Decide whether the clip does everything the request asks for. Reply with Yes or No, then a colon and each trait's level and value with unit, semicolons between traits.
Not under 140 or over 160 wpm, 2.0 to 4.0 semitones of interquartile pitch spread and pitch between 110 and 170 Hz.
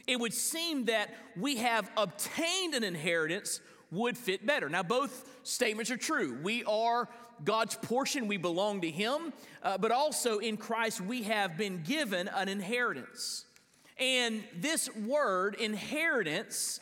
No: average, 145 wpm; average, 3.6 semitones; high, 230 Hz